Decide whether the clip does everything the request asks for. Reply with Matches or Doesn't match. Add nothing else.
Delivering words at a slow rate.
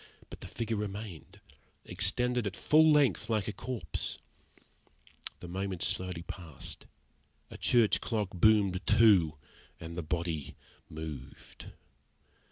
Matches